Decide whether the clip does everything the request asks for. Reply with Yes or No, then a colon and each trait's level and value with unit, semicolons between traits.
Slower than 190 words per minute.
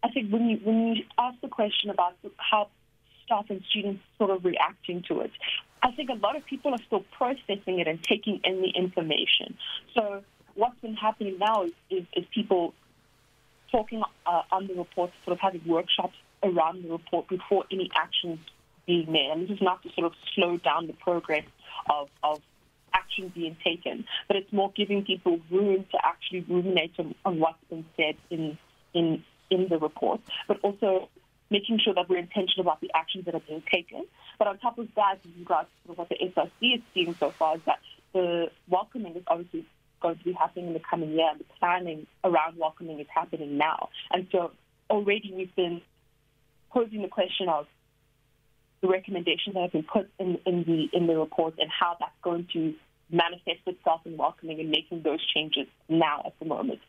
No: average, 195 wpm